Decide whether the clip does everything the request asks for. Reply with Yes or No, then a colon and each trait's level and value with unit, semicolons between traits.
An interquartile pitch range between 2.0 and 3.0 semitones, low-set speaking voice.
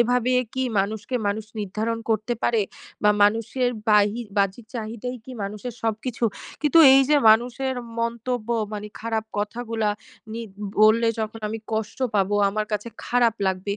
No: narrow, 2.5 semitones; high, 225 Hz